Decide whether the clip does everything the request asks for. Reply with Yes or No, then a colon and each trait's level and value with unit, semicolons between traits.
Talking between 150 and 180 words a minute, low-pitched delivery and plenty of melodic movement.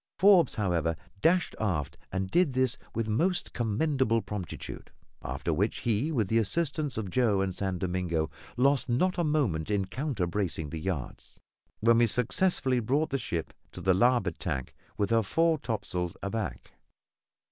Yes: average, 160 wpm; low, 110 Hz; wide, 6.5 semitones